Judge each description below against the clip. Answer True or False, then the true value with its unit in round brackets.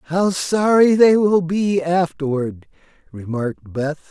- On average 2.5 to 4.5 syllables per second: True (3.6 syllables/s)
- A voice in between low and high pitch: True (170 Hz)